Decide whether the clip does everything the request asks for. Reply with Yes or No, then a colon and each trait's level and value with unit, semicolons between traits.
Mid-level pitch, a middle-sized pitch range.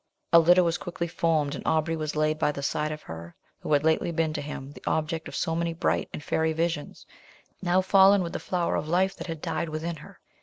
No: medium, 160 Hz; narrow, 1.9 semitones